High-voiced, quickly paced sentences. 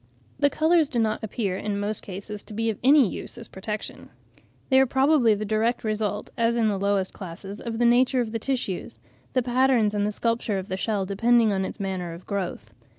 Yes: high, 215 Hz; fast, 215 wpm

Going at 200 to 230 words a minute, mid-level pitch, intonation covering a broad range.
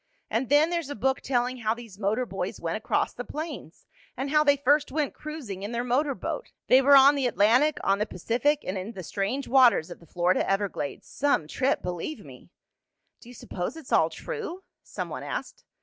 No: fast, 205 wpm; very high, 255 Hz; wide, 6.2 semitones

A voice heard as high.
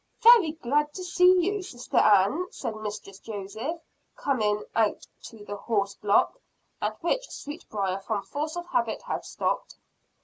Yes: high, 235 Hz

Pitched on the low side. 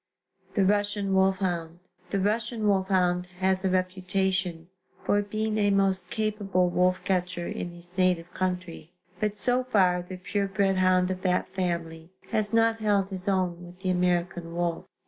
No: medium, 185 Hz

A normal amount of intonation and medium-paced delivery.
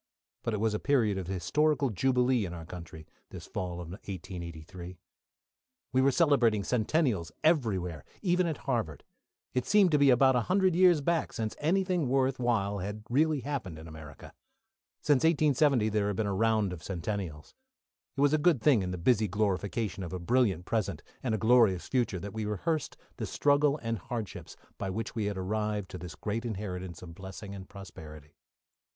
No: wide, 6.4 semitones; average, 180 wpm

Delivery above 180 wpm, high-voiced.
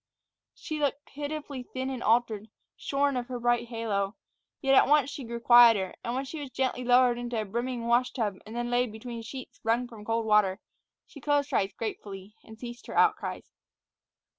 Yes: average, 190 wpm; high, 240 Hz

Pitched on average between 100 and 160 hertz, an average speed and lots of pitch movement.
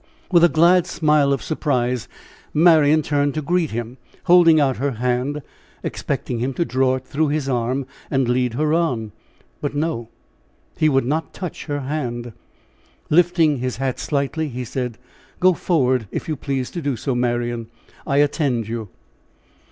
No: medium, 140 Hz; average, 160 wpm; average, 3.9 semitones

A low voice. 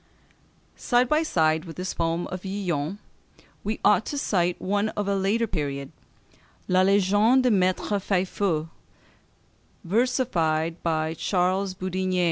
No: medium, 185 Hz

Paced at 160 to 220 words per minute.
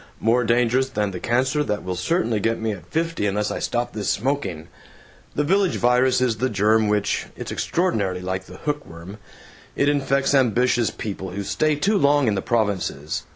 Yes: average, 185 wpm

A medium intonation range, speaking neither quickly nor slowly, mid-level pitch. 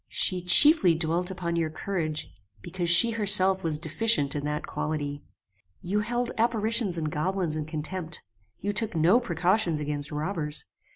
Yes: average, 4.6 semitones; average, 150 wpm; medium, 175 Hz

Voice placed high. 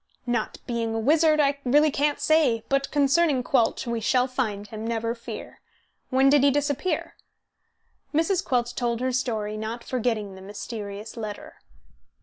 Yes: high, 245 Hz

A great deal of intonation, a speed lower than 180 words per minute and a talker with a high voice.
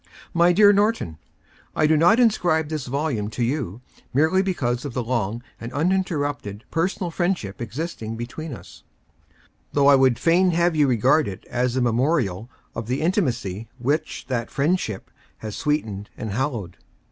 No: wide, 6.1 semitones; average, 160 wpm; low, 135 Hz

